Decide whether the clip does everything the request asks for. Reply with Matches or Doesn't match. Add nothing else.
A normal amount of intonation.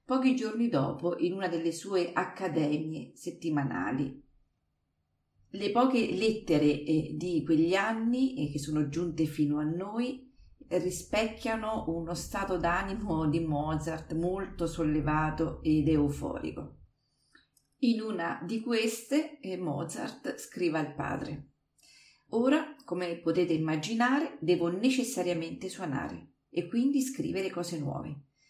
Doesn't match